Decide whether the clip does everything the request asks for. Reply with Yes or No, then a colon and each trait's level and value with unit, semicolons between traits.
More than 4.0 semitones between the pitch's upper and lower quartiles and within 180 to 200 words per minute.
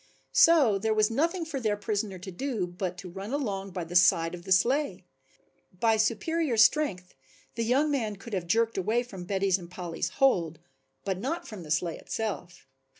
Yes: average, 5.1 semitones; average, 185 wpm